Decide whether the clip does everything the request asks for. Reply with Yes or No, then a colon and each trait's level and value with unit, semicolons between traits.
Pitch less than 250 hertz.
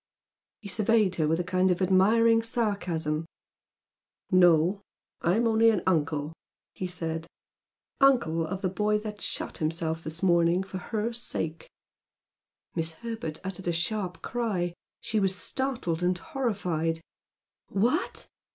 Yes: medium, 185 Hz